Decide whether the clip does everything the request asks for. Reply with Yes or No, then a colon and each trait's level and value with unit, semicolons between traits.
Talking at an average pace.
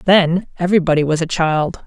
Yes: average, 160 wpm